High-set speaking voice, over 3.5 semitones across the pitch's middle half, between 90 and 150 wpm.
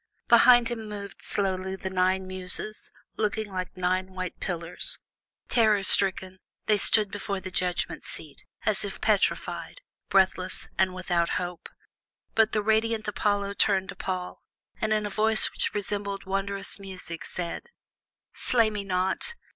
No: high, 195 Hz; narrow, 2.4 semitones; average, 140 wpm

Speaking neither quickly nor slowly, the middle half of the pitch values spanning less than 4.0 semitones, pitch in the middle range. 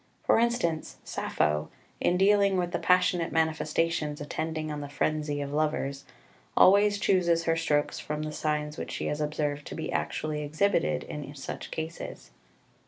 Yes: average, 155 wpm; average, 2.9 semitones; medium, 155 Hz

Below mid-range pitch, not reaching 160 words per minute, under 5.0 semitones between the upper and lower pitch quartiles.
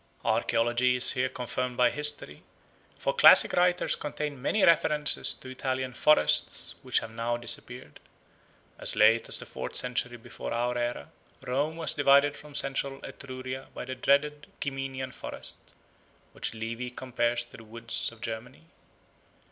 Yes: low, 130 Hz; average, 145 wpm; average, 3.0 semitones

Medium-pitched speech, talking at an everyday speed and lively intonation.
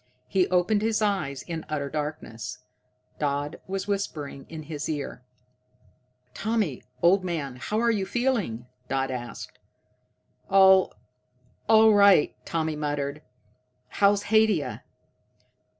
No: medium, 170 Hz; slow, 110 wpm; wide, 5.8 semitones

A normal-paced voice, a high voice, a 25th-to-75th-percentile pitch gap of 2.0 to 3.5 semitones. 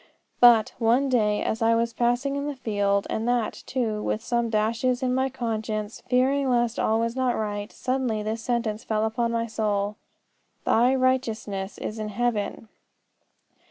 Yes: average, 160 wpm; high, 230 Hz; narrow, 2.6 semitones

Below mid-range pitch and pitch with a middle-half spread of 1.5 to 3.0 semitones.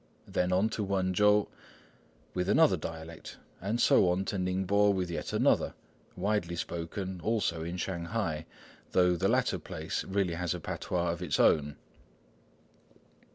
Yes: very low, 90 Hz; average, 2.7 semitones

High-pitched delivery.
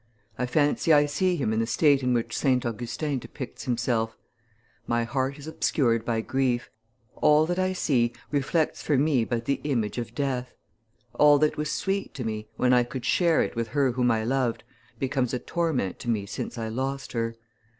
No: low, 130 Hz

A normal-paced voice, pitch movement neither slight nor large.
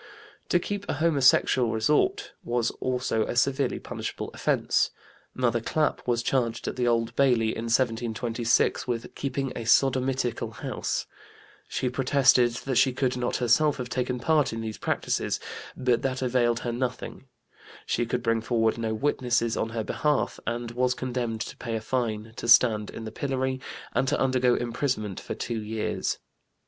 No: average, 160 wpm; narrow, 2.3 semitones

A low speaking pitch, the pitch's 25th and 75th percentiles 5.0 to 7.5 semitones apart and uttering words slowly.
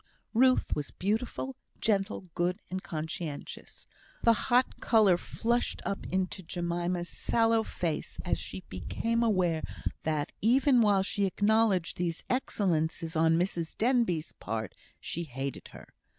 No: medium, 185 Hz; wide, 5.5 semitones; slow, 125 wpm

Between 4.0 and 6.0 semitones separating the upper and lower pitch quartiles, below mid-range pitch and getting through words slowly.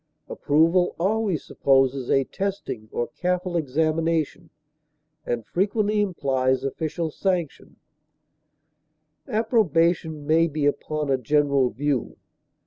No: average, 4.7 semitones; medium, 155 Hz; slow, 95 wpm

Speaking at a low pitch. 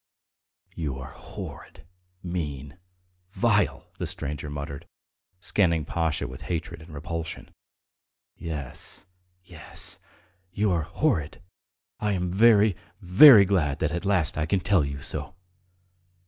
Yes: very low, 85 Hz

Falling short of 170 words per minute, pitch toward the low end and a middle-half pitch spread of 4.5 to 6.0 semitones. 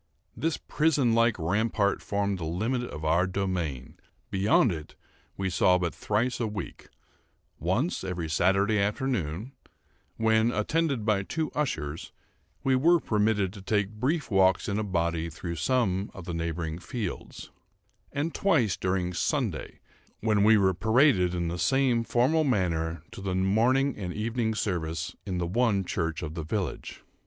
Yes: average, 145 wpm; low, 100 Hz; average, 5.0 semitones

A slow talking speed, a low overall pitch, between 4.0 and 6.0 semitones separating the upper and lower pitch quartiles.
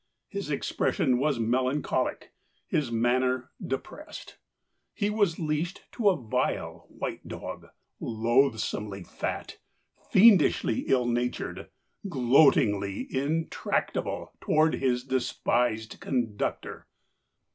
Yes: slow, 90 wpm; low, 130 Hz; average, 4.5 semitones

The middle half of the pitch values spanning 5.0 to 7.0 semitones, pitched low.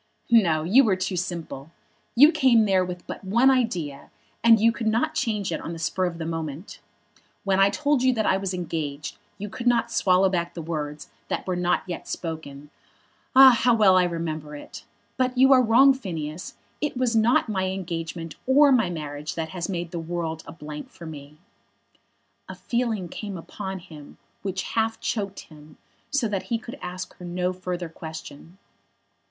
No: wide, 5.6 semitones; medium, 185 Hz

